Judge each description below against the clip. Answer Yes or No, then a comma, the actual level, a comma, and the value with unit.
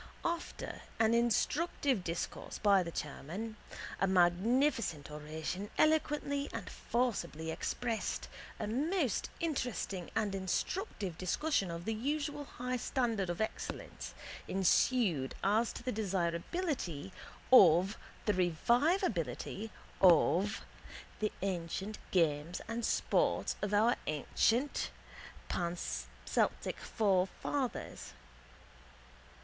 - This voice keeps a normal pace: No, slow, 95 wpm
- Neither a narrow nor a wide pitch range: No, wide, 6.3 semitones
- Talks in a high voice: Yes, high, 205 Hz